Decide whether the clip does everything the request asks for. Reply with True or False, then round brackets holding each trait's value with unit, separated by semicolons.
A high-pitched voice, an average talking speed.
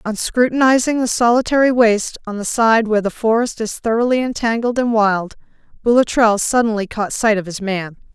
True (225 Hz; 170 wpm)